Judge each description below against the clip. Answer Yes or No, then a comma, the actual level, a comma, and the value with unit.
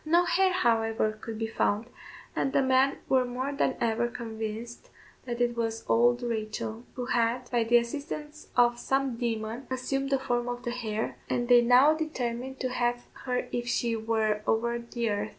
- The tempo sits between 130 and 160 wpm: No, average, 180 wpm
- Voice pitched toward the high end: Yes, high, 240 Hz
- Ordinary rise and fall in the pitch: No, narrow, 2.2 semitones